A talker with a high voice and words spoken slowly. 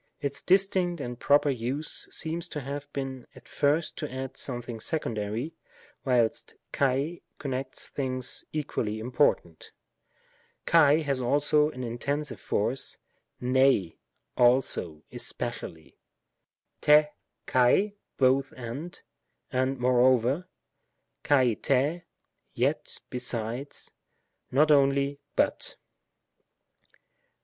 No: low, 135 Hz; slow, 95 wpm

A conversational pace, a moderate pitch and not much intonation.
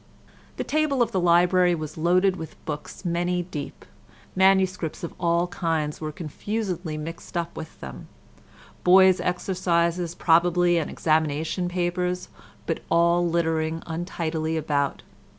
No: slow, 115 wpm; medium, 170 Hz; narrow, 2.0 semitones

